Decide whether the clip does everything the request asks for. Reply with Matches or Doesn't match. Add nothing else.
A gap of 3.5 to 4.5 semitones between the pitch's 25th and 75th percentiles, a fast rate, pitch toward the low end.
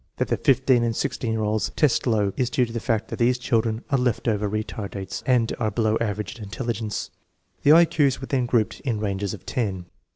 Doesn't match